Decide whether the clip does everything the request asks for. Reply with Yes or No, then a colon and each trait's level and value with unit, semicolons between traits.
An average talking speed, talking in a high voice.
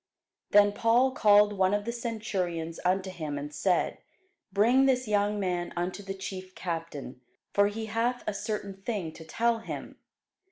Yes: average, 160 wpm; high, 200 Hz